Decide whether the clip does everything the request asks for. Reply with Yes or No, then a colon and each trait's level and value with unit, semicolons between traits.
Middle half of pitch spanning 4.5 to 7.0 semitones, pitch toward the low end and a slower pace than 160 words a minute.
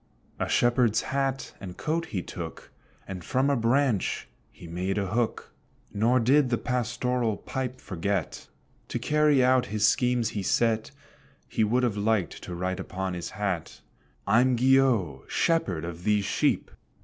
Yes: average, 5.0 semitones; low, 115 Hz; average, 150 wpm